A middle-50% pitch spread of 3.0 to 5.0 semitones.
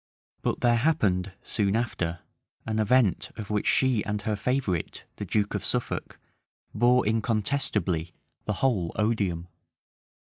Yes: average, 3.8 semitones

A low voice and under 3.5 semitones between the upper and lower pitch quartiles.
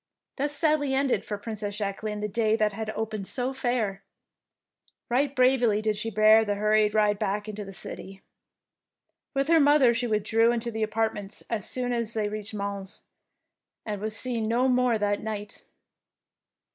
No: high, 220 Hz; average, 2.8 semitones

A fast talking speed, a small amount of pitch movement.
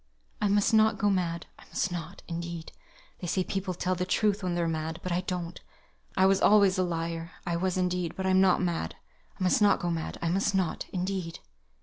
Yes: fast, 215 wpm; narrow, 2.1 semitones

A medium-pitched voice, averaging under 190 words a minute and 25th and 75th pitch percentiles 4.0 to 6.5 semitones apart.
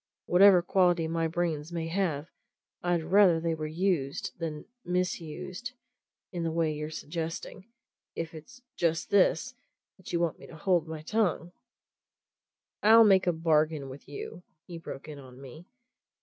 No: medium, 165 Hz; average, 155 wpm; narrow, 2.6 semitones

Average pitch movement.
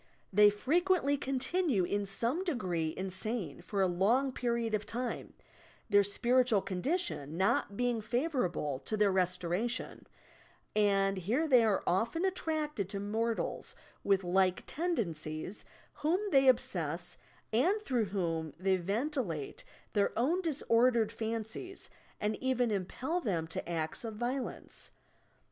No: wide, 5.7 semitones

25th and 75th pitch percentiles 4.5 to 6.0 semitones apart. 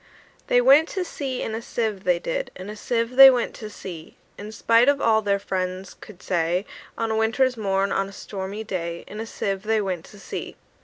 No: average, 3.3 semitones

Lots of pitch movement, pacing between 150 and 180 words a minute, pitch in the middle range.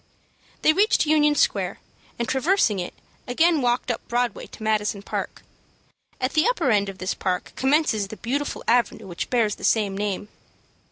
No: wide, 6.1 semitones; average, 165 wpm; high, 240 Hz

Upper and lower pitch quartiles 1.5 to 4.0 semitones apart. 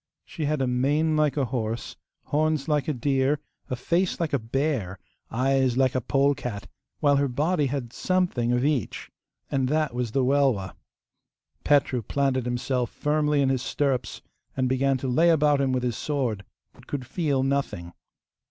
Yes: average, 3.0 semitones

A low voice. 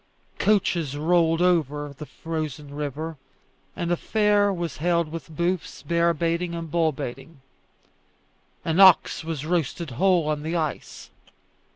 No: medium, 165 Hz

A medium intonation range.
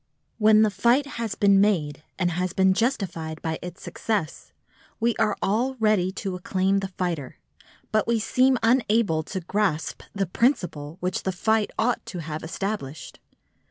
Yes: average, 4.0 semitones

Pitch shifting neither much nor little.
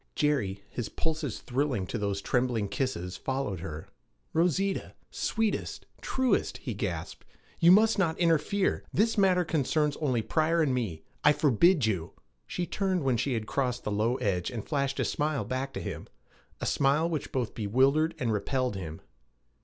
No: wide, 6.7 semitones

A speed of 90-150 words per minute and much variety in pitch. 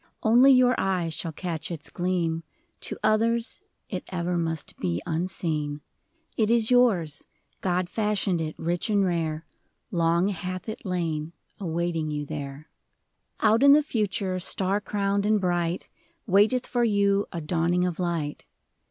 No: average, 145 wpm; average, 4.1 semitones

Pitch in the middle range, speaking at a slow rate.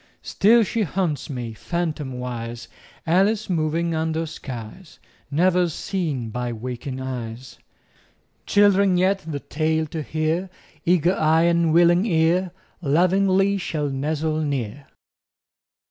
Yes: medium, 160 Hz; slow, 110 wpm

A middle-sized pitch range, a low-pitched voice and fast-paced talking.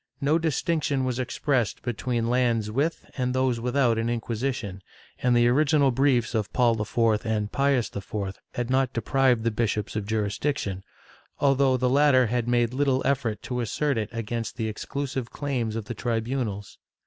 No: average, 3.1 semitones; low, 120 Hz; average, 160 wpm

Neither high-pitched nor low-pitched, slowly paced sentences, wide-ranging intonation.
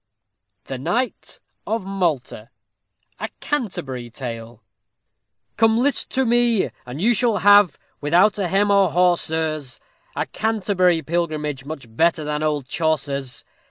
Yes: medium, 170 Hz; slow, 125 wpm; wide, 6.4 semitones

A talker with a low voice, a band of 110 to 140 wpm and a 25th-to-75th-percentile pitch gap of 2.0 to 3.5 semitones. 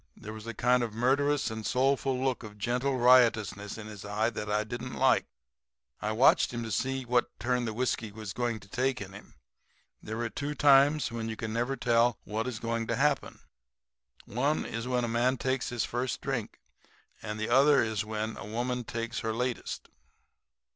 No: low, 120 Hz; average, 195 wpm; narrow, 2.6 semitones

